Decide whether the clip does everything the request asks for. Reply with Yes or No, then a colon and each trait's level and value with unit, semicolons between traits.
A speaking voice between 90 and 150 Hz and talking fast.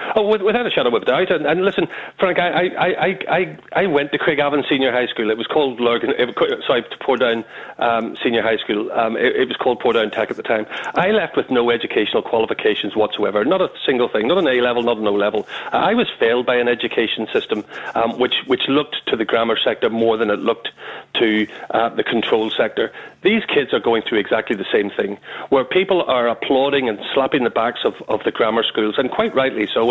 Yes: low, 135 Hz; fast, 230 wpm